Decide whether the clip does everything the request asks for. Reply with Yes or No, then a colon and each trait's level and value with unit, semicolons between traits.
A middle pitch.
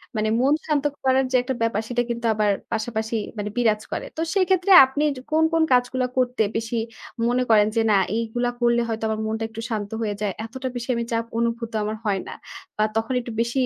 No: high, 235 Hz